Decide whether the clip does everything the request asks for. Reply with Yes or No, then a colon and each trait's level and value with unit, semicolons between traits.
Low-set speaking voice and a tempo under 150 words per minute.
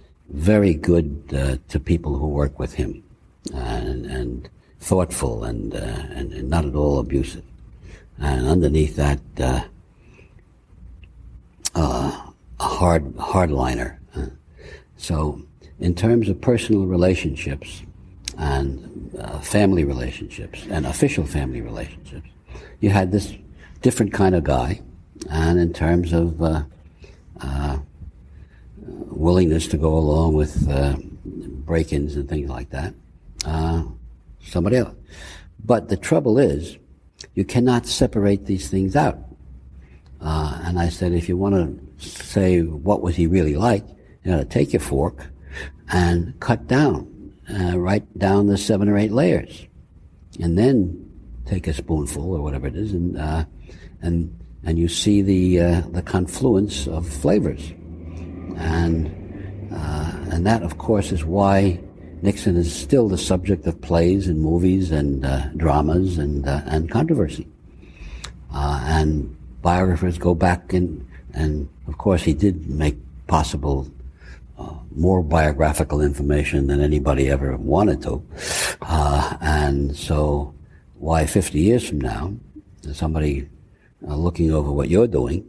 Yes: very low, 80 Hz; slow, 135 wpm